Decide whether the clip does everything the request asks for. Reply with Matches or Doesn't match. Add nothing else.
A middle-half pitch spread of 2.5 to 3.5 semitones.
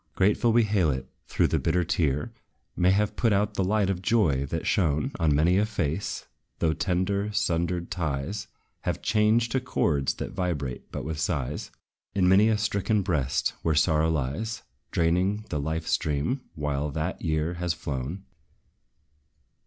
Doesn't match